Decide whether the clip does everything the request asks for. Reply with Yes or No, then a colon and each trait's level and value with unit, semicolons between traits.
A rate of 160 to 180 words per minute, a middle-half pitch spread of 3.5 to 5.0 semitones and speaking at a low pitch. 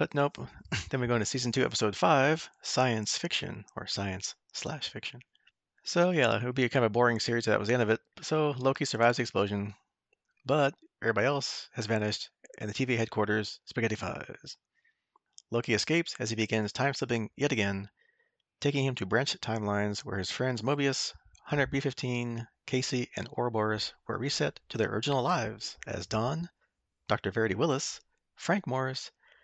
Yes: average, 170 wpm; average, 4.1 semitones; low, 120 Hz